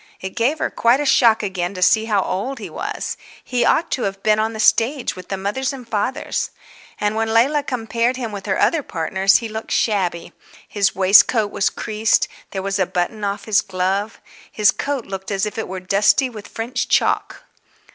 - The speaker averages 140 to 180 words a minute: No, average, 200 wpm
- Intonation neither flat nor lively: Yes, average, 3.1 semitones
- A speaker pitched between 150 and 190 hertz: No, high, 215 Hz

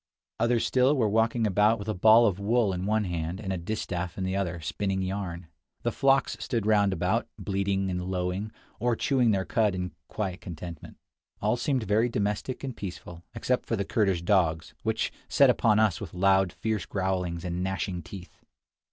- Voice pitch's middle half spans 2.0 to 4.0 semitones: Yes, average, 3.4 semitones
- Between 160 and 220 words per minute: Yes, average, 180 wpm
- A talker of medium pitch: No, low, 100 Hz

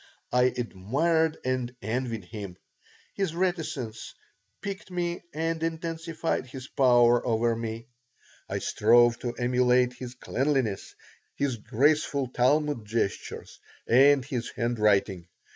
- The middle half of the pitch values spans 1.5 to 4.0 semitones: No, average, 4.6 semitones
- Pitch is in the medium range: No, low, 125 Hz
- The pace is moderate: No, slow, 110 wpm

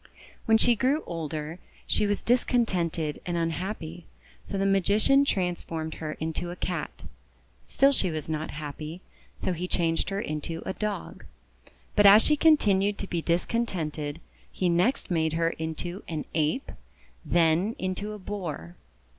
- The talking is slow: No, average, 145 wpm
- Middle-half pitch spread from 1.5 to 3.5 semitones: No, average, 4.3 semitones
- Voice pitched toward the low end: No, medium, 175 Hz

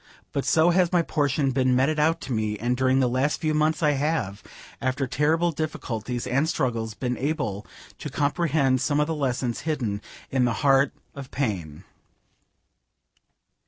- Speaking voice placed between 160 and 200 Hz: No, low, 135 Hz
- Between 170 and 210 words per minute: No, average, 160 wpm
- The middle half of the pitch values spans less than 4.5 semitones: Yes, average, 3.7 semitones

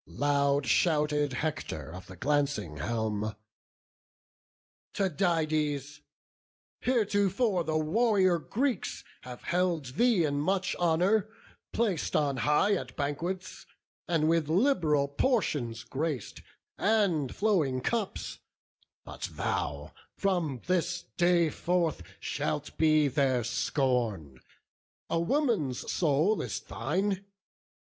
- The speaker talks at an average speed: No, slow, 100 wpm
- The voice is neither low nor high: Yes, medium, 155 Hz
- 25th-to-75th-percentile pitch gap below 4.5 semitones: No, average, 4.9 semitones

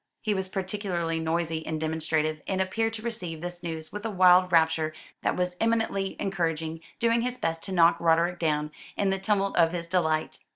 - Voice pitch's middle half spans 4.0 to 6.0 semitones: No, average, 3.1 semitones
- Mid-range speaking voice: Yes, medium, 175 Hz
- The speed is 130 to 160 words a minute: No, average, 190 wpm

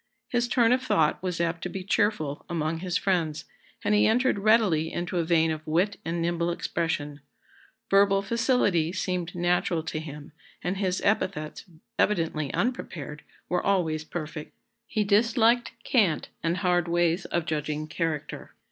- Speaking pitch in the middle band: Yes, medium, 175 Hz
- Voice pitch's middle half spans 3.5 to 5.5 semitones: Yes, average, 4.0 semitones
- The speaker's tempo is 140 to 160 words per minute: Yes, average, 150 wpm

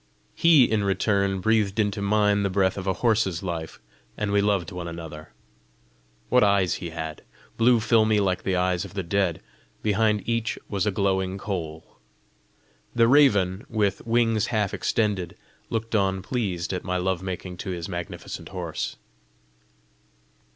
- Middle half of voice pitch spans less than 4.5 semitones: Yes, average, 2.9 semitones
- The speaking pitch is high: No, low, 100 Hz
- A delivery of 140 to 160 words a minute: Yes, average, 150 wpm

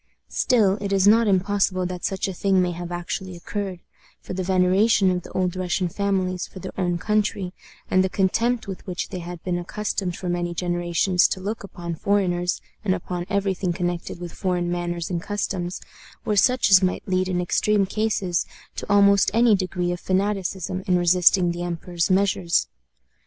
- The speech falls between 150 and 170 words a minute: No, average, 180 wpm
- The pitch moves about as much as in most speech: No, narrow, 2.1 semitones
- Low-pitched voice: No, medium, 185 Hz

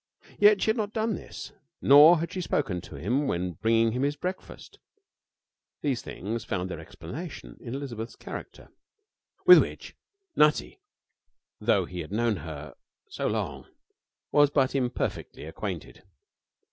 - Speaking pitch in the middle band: No, low, 125 Hz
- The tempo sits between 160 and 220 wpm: No, average, 140 wpm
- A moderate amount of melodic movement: No, wide, 6.9 semitones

